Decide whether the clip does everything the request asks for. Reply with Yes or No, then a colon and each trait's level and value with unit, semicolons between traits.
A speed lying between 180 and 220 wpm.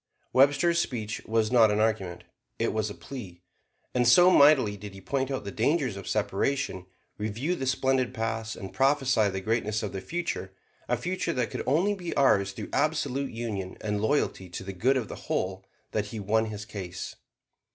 Yes: average, 185 wpm